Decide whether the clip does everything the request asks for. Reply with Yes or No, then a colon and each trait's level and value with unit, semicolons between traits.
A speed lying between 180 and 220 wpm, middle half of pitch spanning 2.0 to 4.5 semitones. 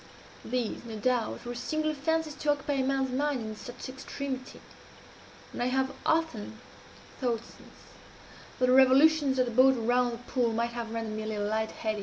Yes: average, 185 wpm; average, 3.0 semitones